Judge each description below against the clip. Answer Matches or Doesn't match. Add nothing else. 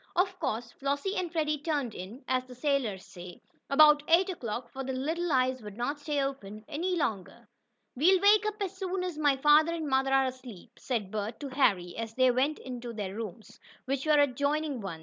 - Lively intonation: Doesn't match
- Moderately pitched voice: Doesn't match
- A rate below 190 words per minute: Doesn't match